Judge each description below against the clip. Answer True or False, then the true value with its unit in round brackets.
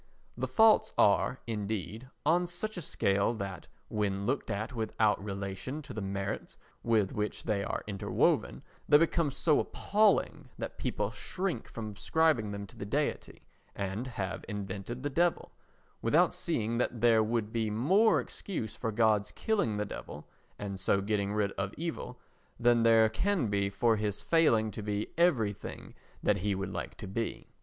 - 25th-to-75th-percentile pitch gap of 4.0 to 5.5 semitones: True (4.5 semitones)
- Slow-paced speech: False (165 wpm)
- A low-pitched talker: True (110 Hz)